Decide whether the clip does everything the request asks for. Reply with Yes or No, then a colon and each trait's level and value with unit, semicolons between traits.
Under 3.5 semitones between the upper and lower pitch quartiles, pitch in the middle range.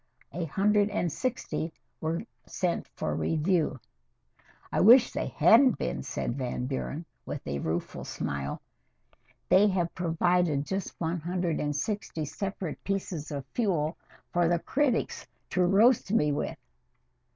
No: average, 4.8 semitones; medium, 175 Hz